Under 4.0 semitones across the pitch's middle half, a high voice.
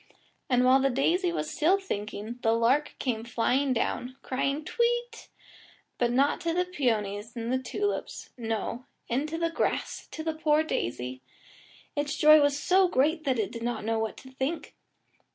No: average, 5.2 semitones; very high, 265 Hz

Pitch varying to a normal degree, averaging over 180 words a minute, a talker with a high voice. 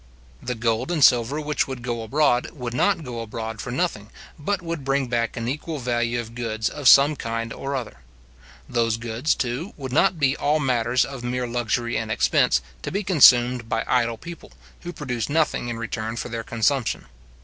No: average, 3.5 semitones; average, 190 wpm; low, 125 Hz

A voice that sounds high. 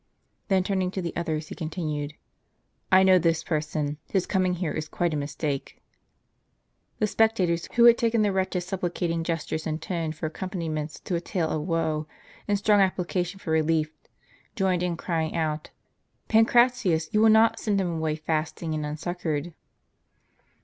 No: medium, 170 Hz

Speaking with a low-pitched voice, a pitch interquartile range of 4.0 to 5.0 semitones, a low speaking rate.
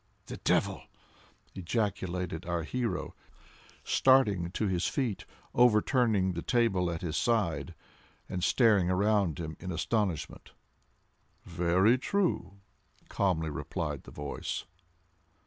Yes: very low, 95 Hz; average, 4.4 semitones; slow, 105 wpm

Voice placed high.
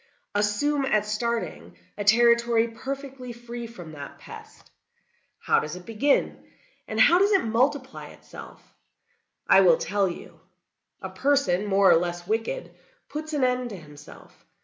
Yes: high, 230 Hz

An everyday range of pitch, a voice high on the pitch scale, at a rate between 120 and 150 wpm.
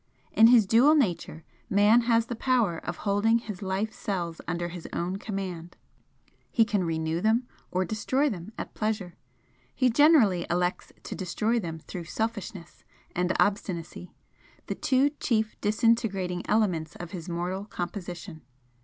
Yes: average, 4.2 semitones; high, 195 Hz; average, 145 wpm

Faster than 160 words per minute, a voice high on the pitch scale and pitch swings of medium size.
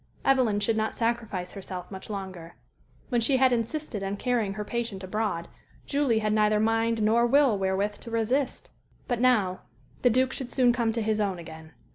Yes: average, 180 wpm; high, 220 Hz; average, 3.4 semitones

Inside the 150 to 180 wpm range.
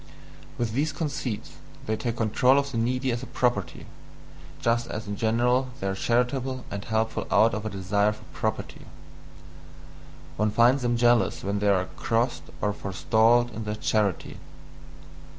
Yes: average, 155 wpm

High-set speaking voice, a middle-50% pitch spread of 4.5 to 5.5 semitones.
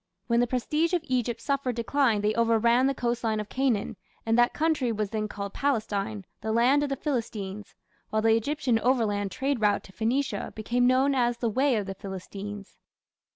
No: high, 235 Hz; average, 3.7 semitones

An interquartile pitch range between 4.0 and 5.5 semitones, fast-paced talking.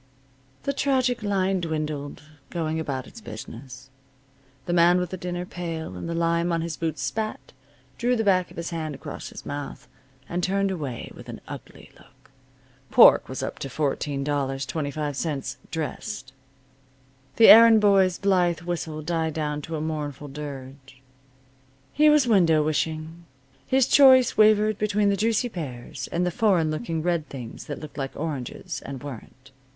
No: average, 5.0 semitones; average, 155 wpm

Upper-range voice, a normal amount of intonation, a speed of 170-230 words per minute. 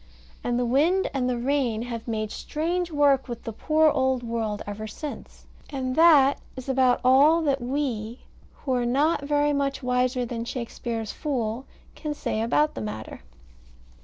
No: very high, 255 Hz; average, 3.7 semitones; average, 160 wpm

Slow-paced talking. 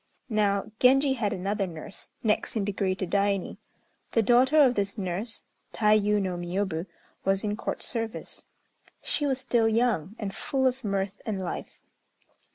No: average, 155 wpm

